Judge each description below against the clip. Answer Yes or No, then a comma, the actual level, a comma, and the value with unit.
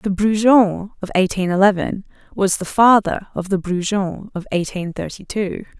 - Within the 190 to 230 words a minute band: No, average, 155 wpm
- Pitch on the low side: No, high, 195 Hz